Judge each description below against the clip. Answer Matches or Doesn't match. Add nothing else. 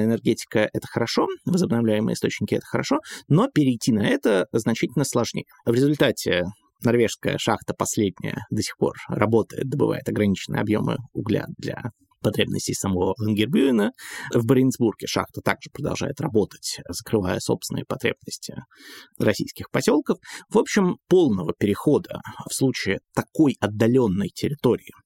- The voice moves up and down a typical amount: Matches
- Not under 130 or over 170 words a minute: Doesn't match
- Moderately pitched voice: Doesn't match